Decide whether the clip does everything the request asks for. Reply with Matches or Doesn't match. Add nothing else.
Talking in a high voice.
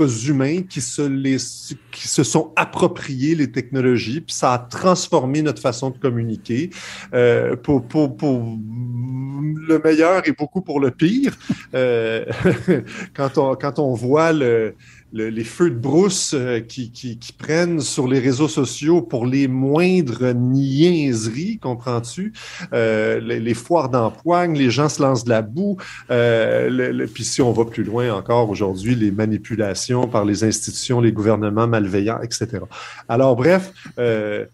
Doesn't match